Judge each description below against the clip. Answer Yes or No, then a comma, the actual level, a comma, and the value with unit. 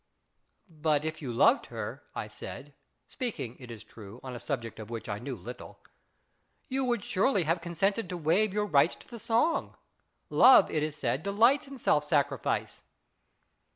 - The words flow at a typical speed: Yes, average, 180 wpm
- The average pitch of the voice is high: No, medium, 155 Hz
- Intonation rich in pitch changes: Yes, wide, 8.5 semitones